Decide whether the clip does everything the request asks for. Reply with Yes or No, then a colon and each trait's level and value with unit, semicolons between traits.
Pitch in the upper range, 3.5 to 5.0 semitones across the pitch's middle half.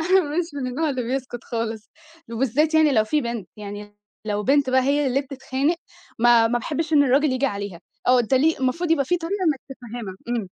Yes: very high, 260 Hz; average, 4.3 semitones